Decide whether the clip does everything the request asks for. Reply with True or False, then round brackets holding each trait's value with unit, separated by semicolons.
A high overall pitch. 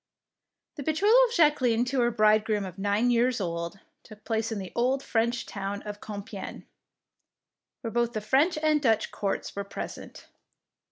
True (225 Hz)